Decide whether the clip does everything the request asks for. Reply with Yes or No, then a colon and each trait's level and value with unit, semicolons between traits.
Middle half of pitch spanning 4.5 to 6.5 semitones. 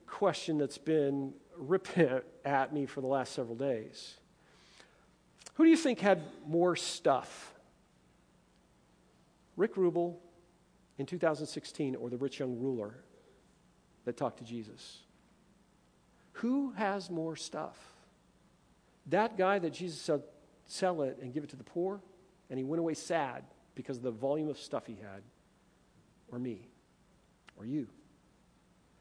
Yes: average, 5.0 semitones